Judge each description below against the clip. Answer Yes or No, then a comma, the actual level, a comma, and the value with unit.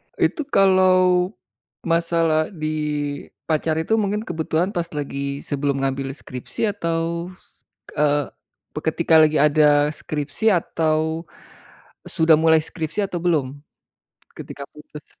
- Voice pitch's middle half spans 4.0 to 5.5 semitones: No, average, 2.8 semitones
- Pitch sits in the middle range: Yes, medium, 160 Hz